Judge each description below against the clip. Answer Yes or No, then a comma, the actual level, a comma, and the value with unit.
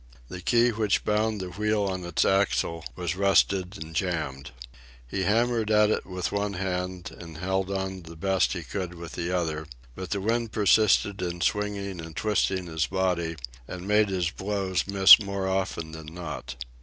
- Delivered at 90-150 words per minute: No, average, 175 wpm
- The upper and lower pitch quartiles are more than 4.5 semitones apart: No, average, 2.8 semitones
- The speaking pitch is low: Yes, very low, 95 Hz